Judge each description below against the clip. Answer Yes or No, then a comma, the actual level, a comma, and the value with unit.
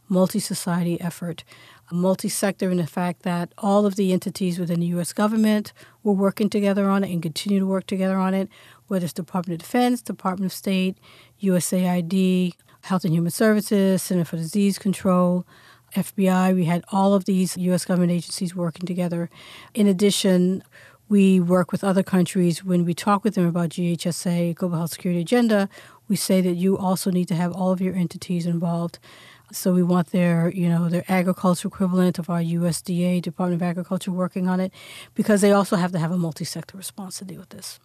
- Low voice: No, medium, 185 Hz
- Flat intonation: Yes, narrow, 1.9 semitones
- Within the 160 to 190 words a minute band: Yes, average, 185 wpm